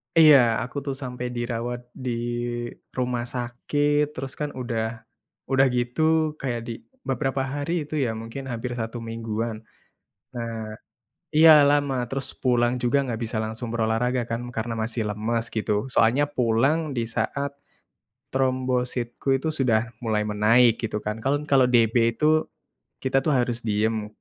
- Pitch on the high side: No, low, 120 Hz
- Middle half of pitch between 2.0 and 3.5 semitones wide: Yes, average, 3.0 semitones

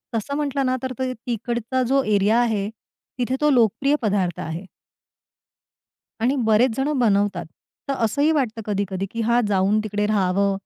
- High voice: Yes, high, 225 Hz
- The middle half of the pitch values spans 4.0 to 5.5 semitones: Yes, average, 4.3 semitones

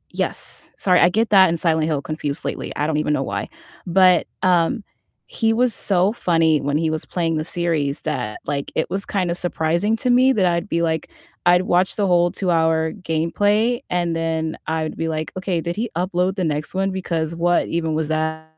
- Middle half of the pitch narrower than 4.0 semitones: Yes, average, 2.8 semitones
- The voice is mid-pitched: Yes, medium, 170 Hz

